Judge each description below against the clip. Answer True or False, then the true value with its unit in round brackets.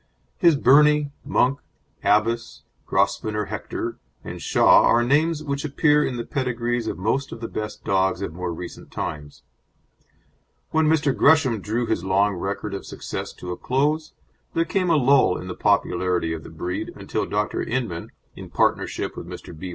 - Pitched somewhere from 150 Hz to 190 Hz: False (115 Hz)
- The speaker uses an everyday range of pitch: False (7.0 semitones)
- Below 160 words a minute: False (165 wpm)